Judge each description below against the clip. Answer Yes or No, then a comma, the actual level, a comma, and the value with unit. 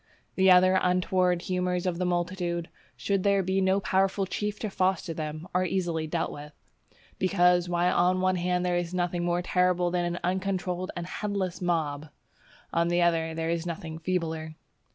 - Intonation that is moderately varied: No, narrow, 1.4 semitones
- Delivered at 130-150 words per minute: No, average, 175 wpm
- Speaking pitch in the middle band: Yes, medium, 180 Hz